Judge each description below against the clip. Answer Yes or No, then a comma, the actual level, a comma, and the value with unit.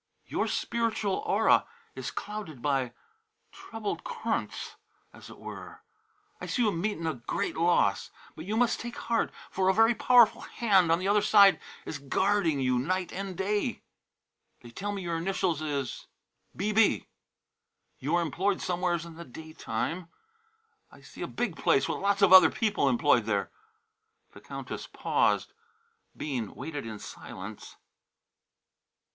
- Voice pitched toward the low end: No, medium, 180 Hz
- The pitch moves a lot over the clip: Yes, wide, 5.9 semitones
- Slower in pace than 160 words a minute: Yes, average, 150 wpm